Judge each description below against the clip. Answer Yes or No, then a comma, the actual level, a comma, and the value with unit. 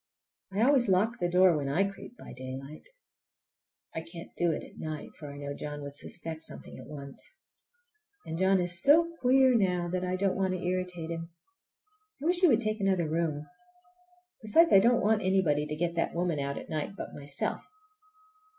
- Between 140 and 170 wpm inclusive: No, average, 190 wpm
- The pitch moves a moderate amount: Yes, average, 4.5 semitones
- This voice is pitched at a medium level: Yes, medium, 180 Hz